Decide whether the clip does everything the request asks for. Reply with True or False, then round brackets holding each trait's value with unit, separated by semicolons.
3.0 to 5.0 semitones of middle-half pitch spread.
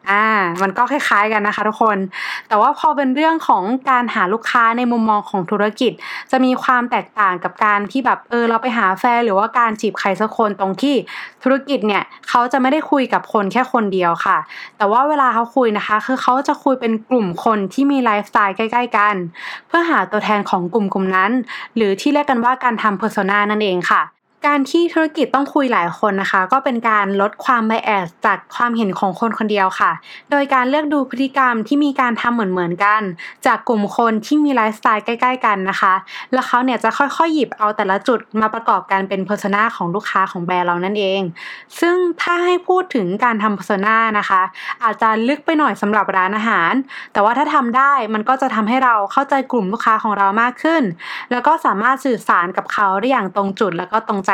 True (4.4 semitones)